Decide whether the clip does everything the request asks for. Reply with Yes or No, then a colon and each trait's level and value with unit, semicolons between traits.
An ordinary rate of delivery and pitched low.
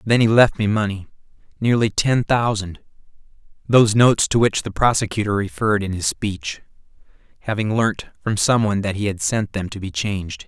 Yes: average, 170 wpm; low, 105 Hz